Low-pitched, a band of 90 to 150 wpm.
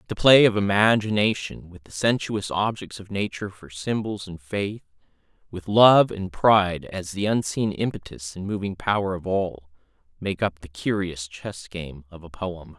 No: very low, 95 Hz; average, 165 wpm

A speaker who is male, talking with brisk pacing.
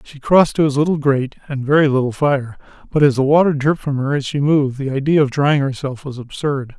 Yes: male; fast, 240 wpm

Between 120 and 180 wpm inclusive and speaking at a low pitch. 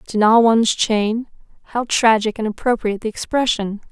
No: average, 140 wpm; high, 225 Hz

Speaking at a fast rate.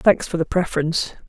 No: average, 190 wpm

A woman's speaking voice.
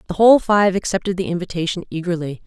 Yes: female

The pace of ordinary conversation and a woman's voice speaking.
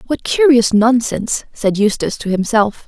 Yes: average, 145 wpm; female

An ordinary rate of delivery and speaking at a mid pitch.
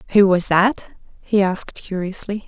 No: average, 145 wpm; high, 195 Hz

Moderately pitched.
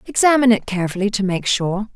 No: high, 210 Hz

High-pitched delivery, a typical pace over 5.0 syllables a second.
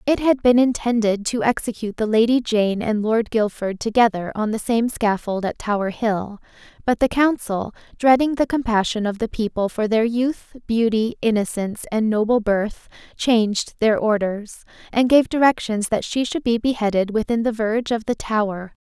No: high, 225 Hz; 4.9 syllables/s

